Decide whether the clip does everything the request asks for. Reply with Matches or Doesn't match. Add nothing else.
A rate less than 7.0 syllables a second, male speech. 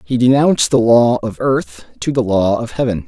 Matches